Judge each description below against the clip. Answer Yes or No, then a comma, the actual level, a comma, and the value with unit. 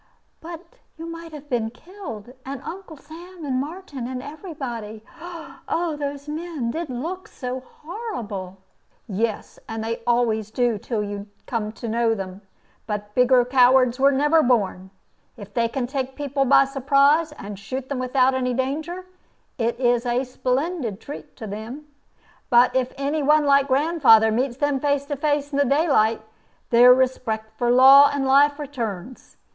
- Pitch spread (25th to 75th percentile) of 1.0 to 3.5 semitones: No, average, 3.9 semitones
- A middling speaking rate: Yes, average, 160 wpm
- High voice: Yes, very high, 260 Hz